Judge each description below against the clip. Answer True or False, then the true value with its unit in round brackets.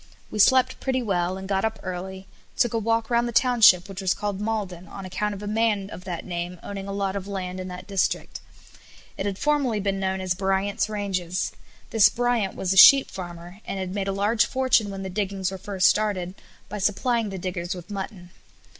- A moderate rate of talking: False (210 wpm)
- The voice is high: True (195 Hz)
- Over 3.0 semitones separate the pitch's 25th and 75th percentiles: False (2.5 semitones)